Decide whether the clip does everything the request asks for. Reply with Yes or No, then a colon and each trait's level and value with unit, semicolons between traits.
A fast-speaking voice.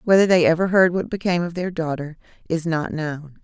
Yes: fast, 210 wpm